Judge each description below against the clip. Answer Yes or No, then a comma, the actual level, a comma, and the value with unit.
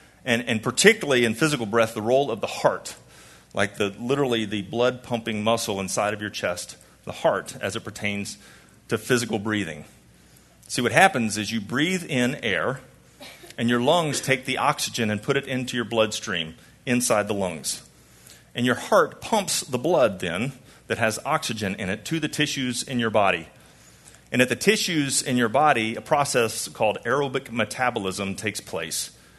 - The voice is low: Yes, low, 115 Hz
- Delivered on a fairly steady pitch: No, average, 3.4 semitones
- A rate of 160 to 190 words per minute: Yes, average, 175 wpm